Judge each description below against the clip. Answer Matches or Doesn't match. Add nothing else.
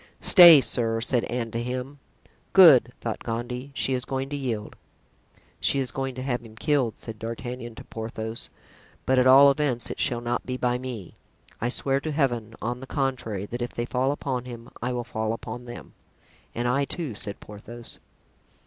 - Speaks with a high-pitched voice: Doesn't match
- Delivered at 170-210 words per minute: Matches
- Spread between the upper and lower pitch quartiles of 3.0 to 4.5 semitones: Doesn't match